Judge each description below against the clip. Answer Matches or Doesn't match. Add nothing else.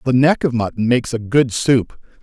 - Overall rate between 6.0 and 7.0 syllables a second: Doesn't match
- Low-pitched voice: Matches